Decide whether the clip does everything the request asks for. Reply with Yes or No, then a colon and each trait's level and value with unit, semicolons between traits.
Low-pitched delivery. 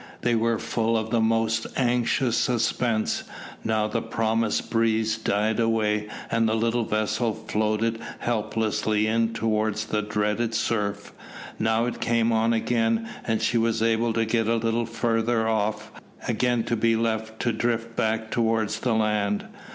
Yes: low, 115 Hz